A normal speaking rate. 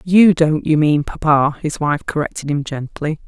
Yes: average, 185 wpm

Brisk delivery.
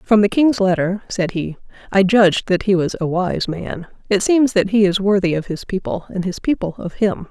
Yes: fast, 230 wpm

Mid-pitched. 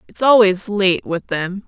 No: high, 200 Hz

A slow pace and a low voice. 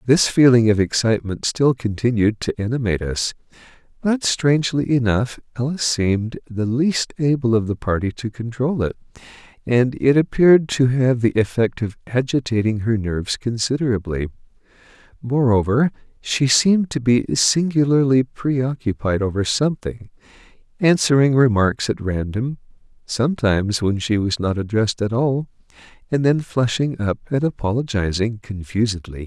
Yes: slow, 125 wpm; low, 120 Hz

